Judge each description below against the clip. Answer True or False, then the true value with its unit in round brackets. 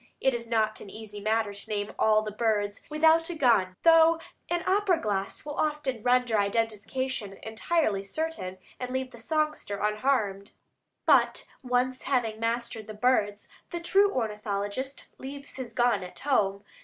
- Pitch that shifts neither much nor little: True (4.8 semitones)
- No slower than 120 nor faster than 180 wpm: True (155 wpm)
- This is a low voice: False (230 Hz)